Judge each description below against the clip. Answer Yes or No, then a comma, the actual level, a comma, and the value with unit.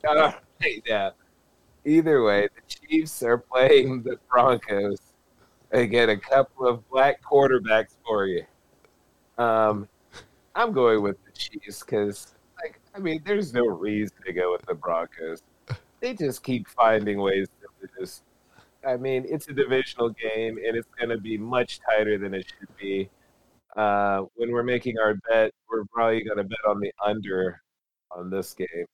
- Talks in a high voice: No, low, 110 Hz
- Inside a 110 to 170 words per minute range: Yes, average, 160 wpm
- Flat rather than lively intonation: No, average, 4.1 semitones